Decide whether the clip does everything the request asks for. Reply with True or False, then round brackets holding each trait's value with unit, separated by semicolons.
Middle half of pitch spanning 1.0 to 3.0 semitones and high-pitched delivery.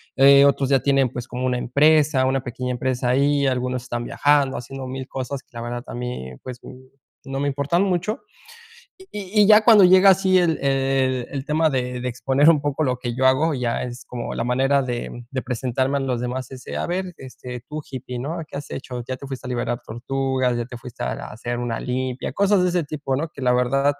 False (2.6 semitones; 130 Hz)